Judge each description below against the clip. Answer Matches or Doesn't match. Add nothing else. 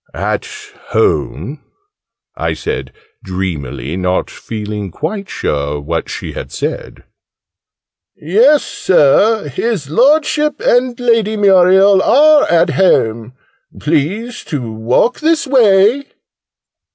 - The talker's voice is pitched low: Doesn't match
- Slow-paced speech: Matches